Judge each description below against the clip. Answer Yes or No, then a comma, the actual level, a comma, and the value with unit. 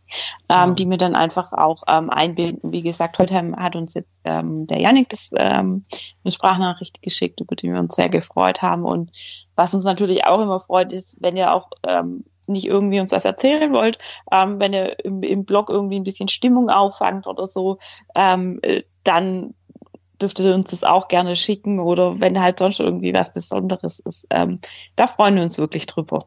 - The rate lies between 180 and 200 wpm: Yes, fast, 190 wpm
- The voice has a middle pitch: Yes, medium, 180 Hz